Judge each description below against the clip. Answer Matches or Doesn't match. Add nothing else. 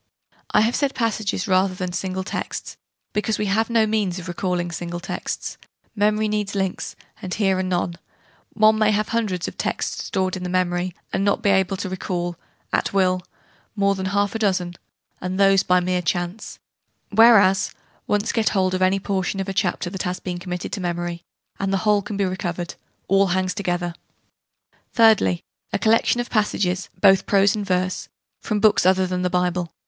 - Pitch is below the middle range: Doesn't match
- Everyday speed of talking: Matches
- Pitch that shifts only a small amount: Matches